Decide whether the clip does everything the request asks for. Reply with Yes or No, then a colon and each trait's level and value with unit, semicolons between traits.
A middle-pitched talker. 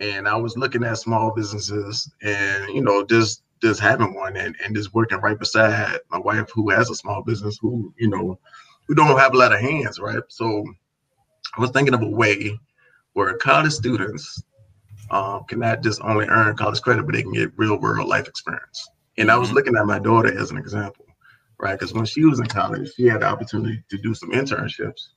No: low, 110 Hz